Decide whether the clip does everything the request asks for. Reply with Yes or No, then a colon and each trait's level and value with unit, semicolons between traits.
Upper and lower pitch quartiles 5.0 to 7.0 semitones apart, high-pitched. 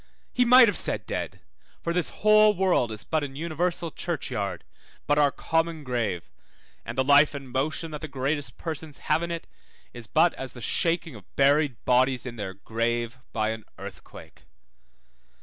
No: wide, 5.5 semitones; medium, 140 Hz